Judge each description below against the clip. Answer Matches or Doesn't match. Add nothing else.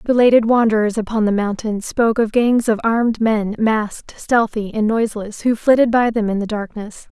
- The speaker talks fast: Doesn't match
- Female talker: Matches